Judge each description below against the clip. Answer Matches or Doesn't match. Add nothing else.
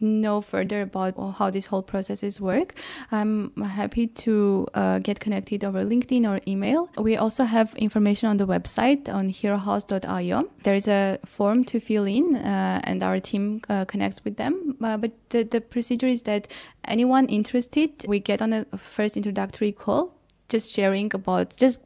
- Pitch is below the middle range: Doesn't match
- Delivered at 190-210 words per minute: Doesn't match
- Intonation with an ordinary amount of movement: Matches